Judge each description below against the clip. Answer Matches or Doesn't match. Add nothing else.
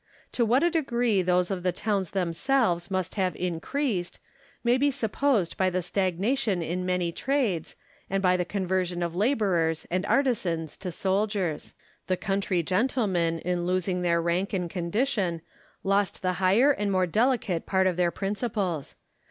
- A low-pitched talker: Doesn't match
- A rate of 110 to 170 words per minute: Matches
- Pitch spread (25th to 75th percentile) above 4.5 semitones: Doesn't match